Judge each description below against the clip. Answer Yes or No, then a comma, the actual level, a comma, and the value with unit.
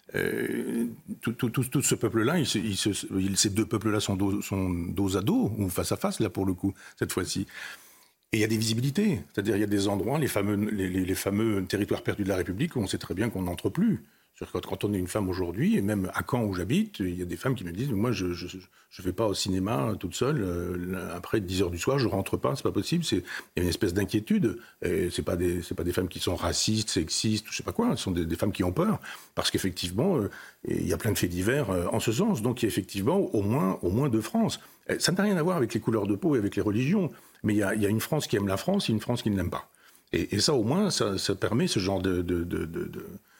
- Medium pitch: No, low, 100 Hz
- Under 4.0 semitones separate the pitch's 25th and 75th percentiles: Yes, average, 3.4 semitones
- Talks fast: Yes, fast, 285 wpm